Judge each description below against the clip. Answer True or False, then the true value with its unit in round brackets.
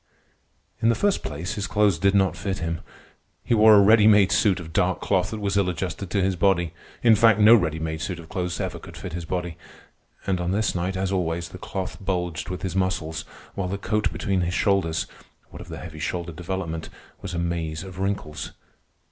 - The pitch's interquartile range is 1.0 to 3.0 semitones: True (2.6 semitones)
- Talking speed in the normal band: False (215 wpm)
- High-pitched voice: False (95 Hz)